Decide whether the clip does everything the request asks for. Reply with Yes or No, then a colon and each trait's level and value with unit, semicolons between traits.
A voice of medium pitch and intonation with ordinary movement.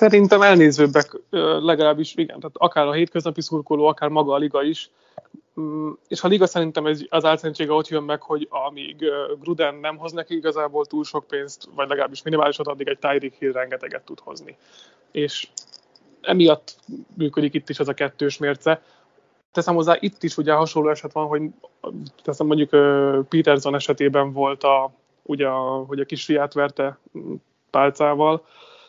No: medium, 150 Hz; narrow, 2.3 semitones